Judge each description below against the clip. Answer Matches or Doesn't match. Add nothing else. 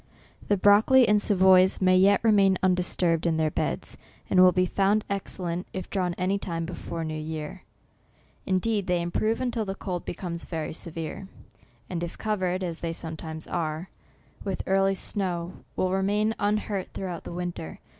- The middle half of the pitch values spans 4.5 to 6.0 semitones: Doesn't match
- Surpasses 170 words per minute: Doesn't match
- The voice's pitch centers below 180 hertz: Doesn't match